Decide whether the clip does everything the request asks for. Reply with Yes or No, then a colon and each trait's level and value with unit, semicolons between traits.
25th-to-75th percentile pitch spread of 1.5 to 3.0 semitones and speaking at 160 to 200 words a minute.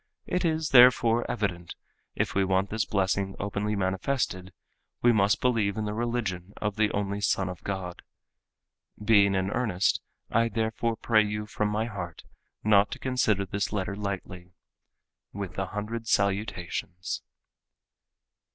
No: narrow, 2.6 semitones; average, 140 wpm